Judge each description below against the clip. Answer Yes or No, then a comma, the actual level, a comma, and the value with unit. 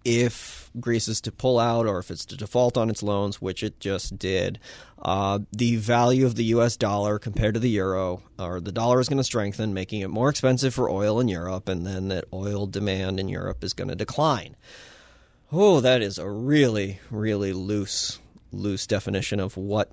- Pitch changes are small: No, average, 3.5 semitones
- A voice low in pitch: Yes, low, 105 Hz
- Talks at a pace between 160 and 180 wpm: No, average, 200 wpm